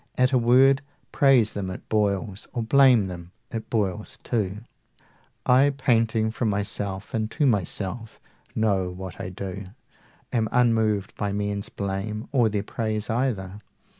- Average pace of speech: Yes, average, 145 wpm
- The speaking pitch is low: Yes, low, 110 Hz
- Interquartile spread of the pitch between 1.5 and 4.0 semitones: Yes, average, 3.2 semitones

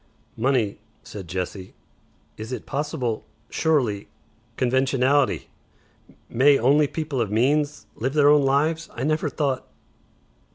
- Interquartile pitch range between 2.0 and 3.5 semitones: No, average, 4.0 semitones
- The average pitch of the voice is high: No, low, 135 Hz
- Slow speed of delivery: Yes, slow, 115 wpm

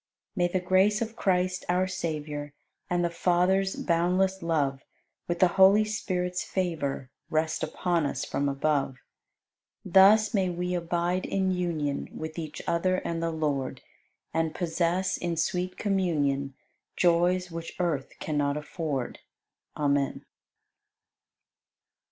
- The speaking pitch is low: No, medium, 175 Hz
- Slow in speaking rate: Yes, slow, 125 wpm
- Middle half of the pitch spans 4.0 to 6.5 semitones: No, average, 3.2 semitones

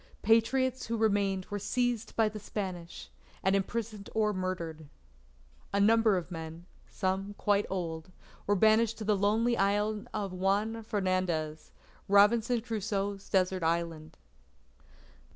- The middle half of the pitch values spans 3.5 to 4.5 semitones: No, average, 2.9 semitones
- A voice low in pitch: No, high, 200 Hz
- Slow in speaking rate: Yes, slow, 125 wpm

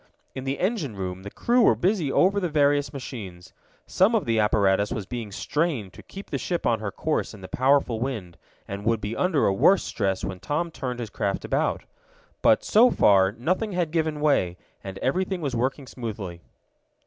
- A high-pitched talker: No, low, 130 Hz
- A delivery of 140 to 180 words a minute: No, average, 195 wpm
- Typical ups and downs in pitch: No, wide, 8.3 semitones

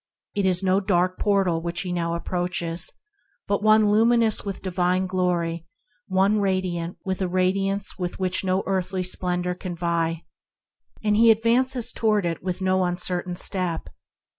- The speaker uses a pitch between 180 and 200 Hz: Yes, medium, 185 Hz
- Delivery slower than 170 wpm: Yes, average, 150 wpm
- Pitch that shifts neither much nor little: No, narrow, 2.0 semitones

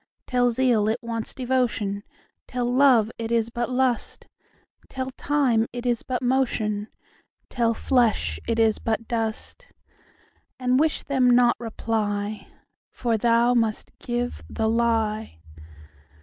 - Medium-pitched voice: No, high, 235 Hz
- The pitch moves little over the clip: Yes, narrow, 2.1 semitones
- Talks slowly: Yes, slow, 105 wpm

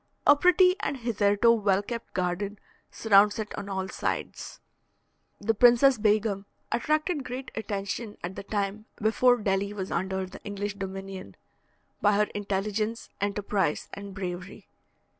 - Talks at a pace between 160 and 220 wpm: No, slow, 135 wpm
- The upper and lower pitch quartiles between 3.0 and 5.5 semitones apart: No, narrow, 2.5 semitones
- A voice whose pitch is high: Yes, high, 205 Hz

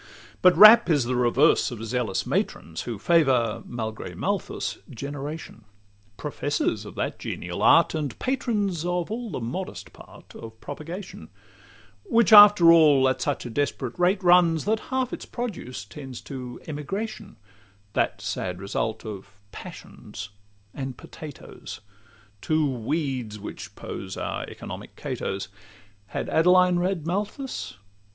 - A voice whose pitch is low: No, medium, 150 Hz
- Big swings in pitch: Yes, wide, 7.1 semitones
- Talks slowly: Yes, slow, 130 wpm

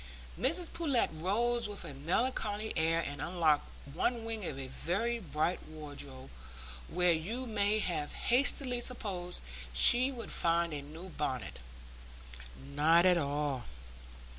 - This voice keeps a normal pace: No, slow, 130 wpm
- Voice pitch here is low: No, medium, 175 Hz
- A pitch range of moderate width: No, wide, 7.3 semitones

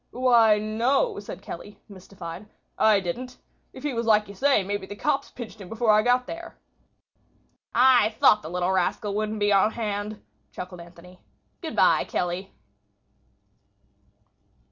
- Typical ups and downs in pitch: Yes, average, 4.0 semitones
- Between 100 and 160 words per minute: Yes, average, 145 wpm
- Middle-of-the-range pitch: No, high, 210 Hz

